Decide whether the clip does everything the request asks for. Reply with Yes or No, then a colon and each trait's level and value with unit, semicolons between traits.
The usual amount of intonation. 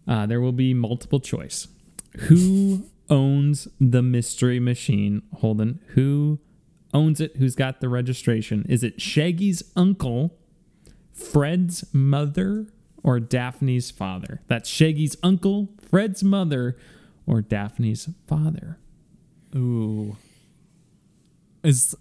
No: wide, 5.9 semitones